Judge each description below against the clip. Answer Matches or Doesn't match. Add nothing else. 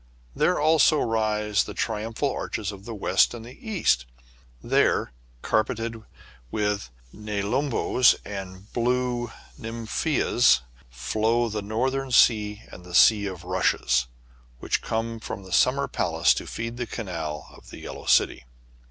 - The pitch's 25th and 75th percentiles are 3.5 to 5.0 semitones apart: Doesn't match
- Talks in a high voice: Doesn't match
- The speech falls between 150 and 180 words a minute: Doesn't match